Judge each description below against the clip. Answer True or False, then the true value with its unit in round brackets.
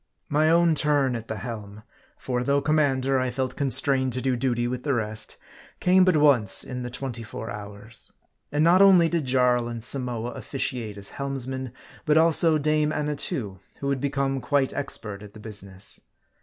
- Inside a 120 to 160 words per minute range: False (175 wpm)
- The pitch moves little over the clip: False (3.9 semitones)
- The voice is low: True (130 Hz)